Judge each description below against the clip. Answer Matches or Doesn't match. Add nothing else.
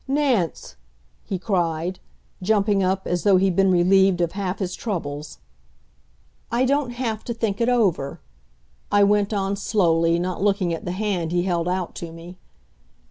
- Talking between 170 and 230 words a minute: Doesn't match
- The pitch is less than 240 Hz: Matches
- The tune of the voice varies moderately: Matches